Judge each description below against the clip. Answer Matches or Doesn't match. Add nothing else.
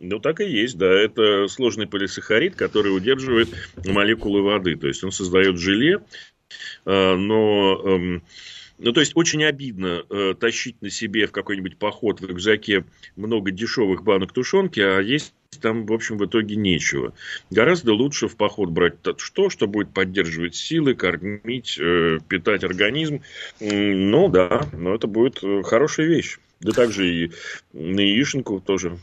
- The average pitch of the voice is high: Doesn't match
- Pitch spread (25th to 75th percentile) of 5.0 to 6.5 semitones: Doesn't match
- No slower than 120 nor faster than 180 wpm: Matches